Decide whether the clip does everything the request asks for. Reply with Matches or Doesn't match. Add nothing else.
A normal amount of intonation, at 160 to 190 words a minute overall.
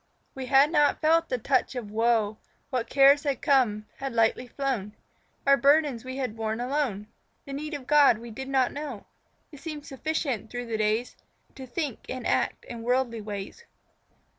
Matches